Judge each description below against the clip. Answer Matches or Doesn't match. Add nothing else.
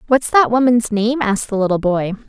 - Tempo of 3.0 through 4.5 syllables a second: Doesn't match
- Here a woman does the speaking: Matches